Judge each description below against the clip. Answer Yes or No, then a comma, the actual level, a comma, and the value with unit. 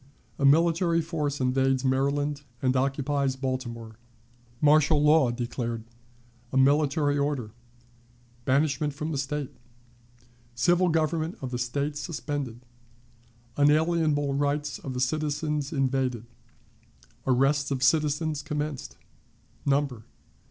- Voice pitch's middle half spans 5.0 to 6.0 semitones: No, narrow, 2.4 semitones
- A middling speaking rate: No, slow, 100 wpm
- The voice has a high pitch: No, medium, 145 Hz